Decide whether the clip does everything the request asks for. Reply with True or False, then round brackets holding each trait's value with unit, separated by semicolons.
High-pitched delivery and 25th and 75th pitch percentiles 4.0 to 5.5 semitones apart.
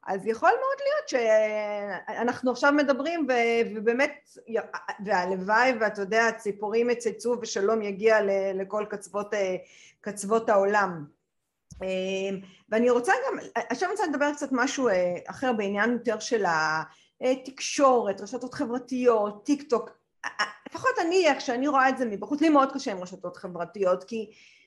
True (225 Hz; 4.6 semitones)